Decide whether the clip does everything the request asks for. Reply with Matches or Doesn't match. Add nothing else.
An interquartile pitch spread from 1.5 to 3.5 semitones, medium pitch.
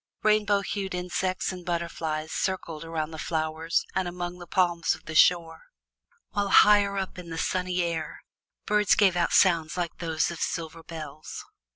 Matches